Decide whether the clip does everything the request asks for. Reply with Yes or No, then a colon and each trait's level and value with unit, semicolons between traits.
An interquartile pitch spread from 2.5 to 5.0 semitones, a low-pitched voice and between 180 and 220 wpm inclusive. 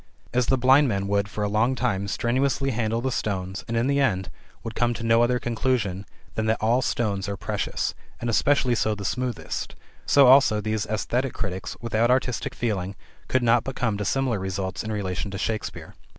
Yes: average, 3.7 semitones; low, 115 Hz; average, 195 wpm